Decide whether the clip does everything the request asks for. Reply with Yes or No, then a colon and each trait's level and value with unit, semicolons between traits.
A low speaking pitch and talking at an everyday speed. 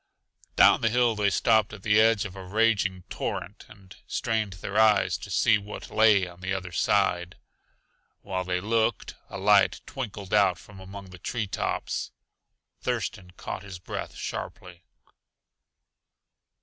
Yes: low, 100 Hz; average, 150 wpm